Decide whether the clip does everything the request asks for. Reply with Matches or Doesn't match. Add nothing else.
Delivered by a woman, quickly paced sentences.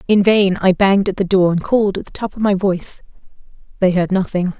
Matches